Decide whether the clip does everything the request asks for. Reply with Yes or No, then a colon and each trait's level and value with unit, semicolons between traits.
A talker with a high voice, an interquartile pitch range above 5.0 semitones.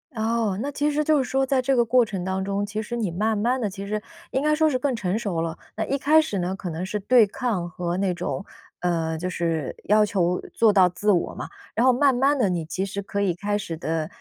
Yes: high, 205 Hz; wide, 5.6 semitones